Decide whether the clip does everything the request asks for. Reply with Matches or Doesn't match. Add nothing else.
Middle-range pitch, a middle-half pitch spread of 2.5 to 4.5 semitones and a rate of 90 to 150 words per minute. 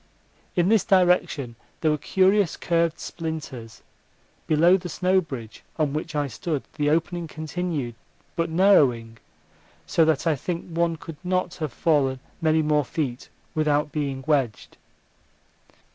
Matches